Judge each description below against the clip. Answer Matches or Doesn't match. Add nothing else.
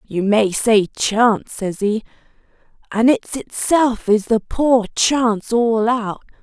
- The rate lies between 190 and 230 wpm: Doesn't match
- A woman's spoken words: Matches